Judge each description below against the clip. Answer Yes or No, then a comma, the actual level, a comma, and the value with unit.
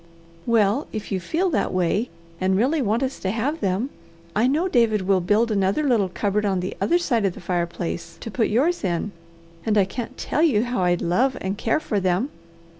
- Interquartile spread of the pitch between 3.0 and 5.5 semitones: Yes, average, 5.1 semitones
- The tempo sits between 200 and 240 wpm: Yes, fast, 205 wpm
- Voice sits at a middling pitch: No, high, 215 Hz